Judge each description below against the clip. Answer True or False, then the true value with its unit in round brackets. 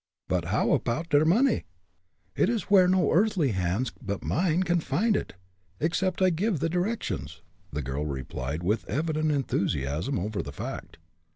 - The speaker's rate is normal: True (160 wpm)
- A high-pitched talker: False (155 Hz)